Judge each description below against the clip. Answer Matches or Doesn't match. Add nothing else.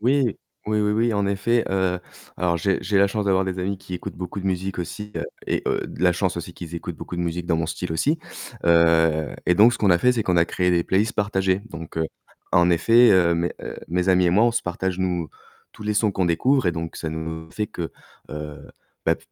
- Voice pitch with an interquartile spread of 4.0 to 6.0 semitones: Doesn't match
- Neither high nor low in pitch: Doesn't match